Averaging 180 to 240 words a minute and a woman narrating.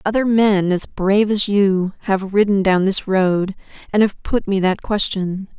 Yes: average, 185 wpm; female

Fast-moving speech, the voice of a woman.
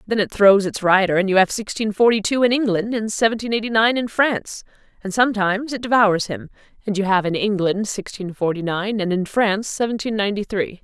Yes: fast, 210 wpm; female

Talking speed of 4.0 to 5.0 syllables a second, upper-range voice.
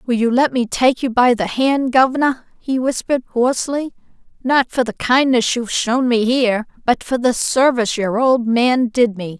Yes: 4.9 syllables/s; high, 245 Hz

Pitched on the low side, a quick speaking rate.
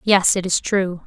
No: medium, 185 Hz; fast, 225 wpm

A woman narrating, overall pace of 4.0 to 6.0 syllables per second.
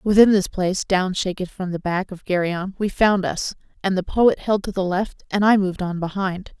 Yes: female; 5.0 syllables/s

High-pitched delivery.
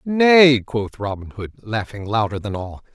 No: low, 115 Hz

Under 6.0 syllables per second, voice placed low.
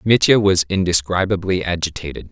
Yes: 5.4 syllables/s; very low, 95 Hz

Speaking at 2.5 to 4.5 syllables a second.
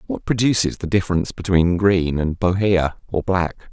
No: 5.1 syllables/s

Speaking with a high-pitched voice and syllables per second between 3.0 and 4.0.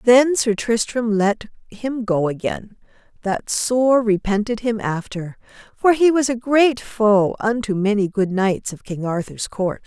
Yes: high, 220 Hz; 3.9 syllables/s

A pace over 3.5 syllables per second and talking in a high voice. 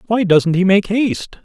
Yes: 4.7 syllables/s; high, 200 Hz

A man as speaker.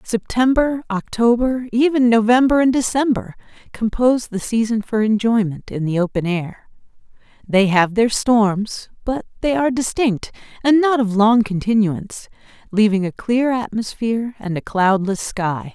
No: female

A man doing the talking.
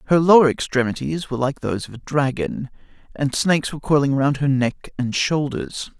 Yes: male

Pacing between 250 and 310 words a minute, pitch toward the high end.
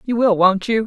Yes: fast, 275 wpm; high, 215 Hz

